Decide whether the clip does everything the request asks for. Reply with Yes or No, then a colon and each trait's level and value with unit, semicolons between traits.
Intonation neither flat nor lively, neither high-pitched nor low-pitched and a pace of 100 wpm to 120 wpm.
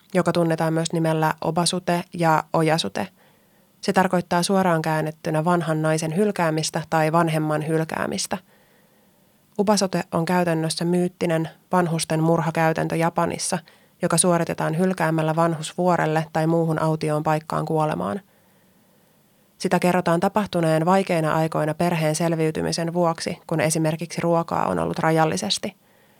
No: narrow, 2.0 semitones; medium, 170 Hz; average, 110 wpm